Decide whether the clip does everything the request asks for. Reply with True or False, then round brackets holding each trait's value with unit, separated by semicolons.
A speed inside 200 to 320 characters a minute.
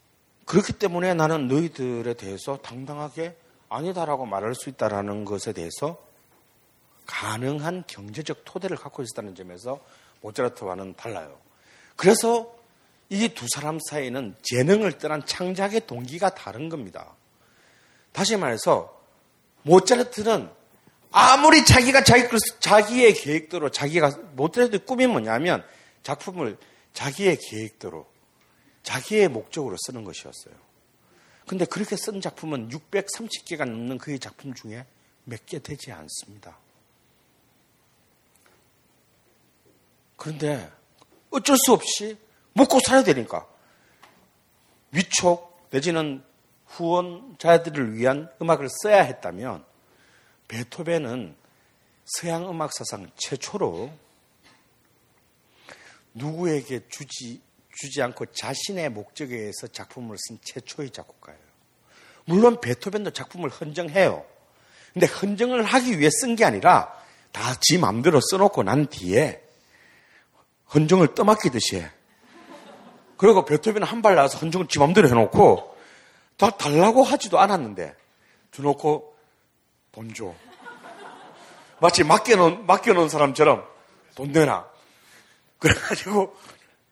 True (250 characters per minute)